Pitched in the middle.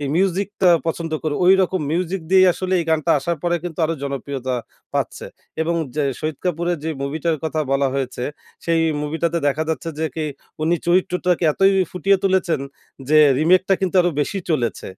Yes: medium, 170 Hz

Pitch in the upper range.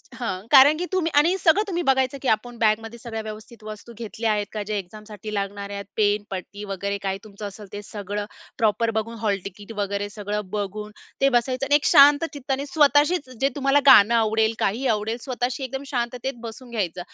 Yes: high, 225 Hz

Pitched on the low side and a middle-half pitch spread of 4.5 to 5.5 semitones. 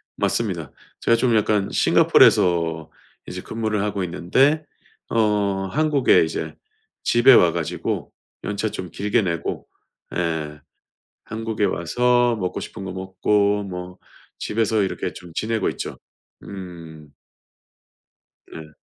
No: low, 100 Hz; average, 4.0 semitones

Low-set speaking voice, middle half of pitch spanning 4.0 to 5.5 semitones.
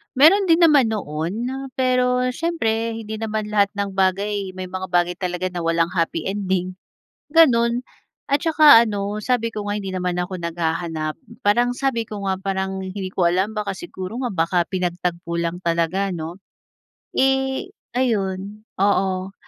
No: high, 195 Hz; average, 4.5 semitones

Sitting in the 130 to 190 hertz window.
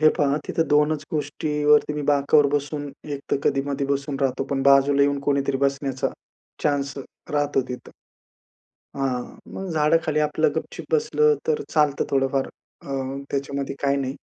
Yes: medium, 140 Hz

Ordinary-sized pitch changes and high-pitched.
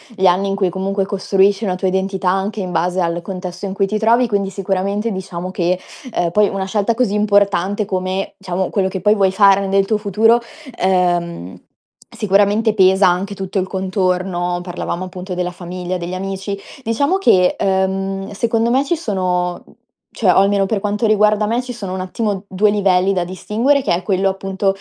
No: narrow, 1.9 semitones; high, 195 Hz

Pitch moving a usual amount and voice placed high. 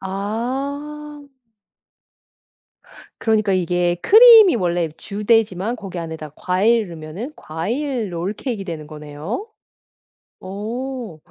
No: wide, 6.2 semitones; high, 205 Hz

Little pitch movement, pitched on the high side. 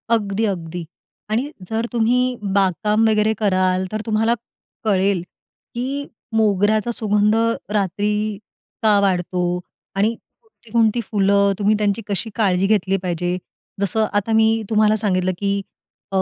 Yes: narrow, 2.3 semitones; high, 205 Hz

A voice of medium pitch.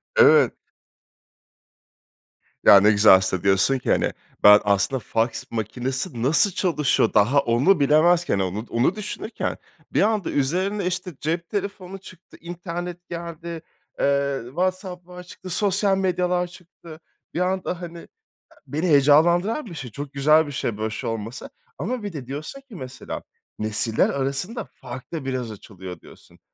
Yes: medium, 155 Hz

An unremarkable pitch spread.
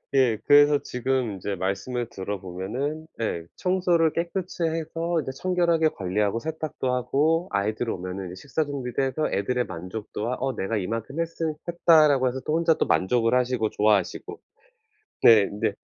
No: wide, 7.2 semitones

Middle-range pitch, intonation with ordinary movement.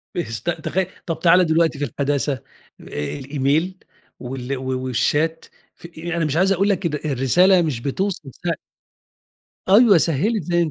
Yes: medium, 160 Hz; average, 4.4 semitones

